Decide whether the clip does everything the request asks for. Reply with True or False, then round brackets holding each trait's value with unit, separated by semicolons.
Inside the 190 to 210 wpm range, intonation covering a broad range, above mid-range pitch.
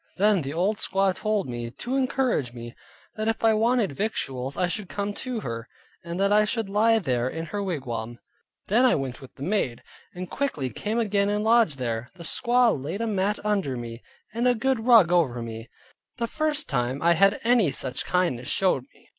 True (200 wpm; 8.8 semitones; 195 Hz)